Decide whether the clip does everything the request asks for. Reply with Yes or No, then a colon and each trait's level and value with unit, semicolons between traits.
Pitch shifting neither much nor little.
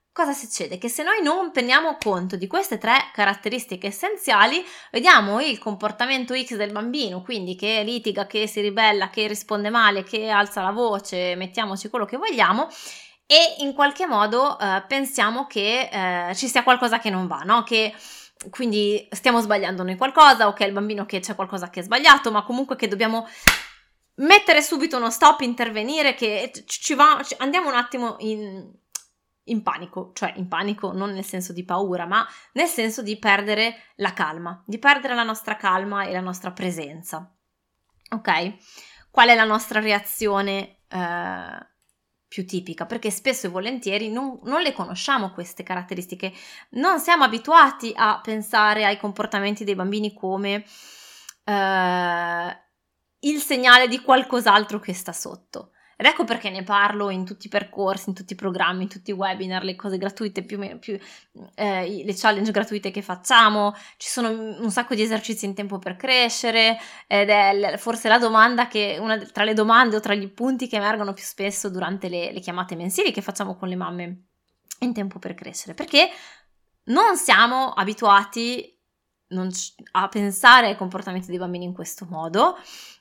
Yes: average, 3.8 semitones